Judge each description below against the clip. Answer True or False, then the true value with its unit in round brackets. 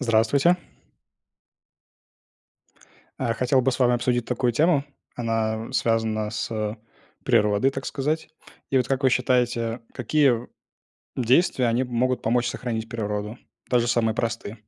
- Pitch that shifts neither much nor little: False (2.3 semitones)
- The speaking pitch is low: True (120 Hz)